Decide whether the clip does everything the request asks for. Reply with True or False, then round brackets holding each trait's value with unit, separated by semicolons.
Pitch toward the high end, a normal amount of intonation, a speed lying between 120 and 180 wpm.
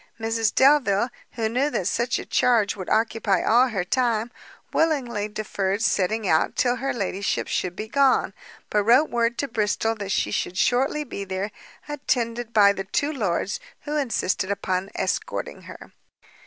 True (225 Hz; 3.8 semitones; 160 wpm)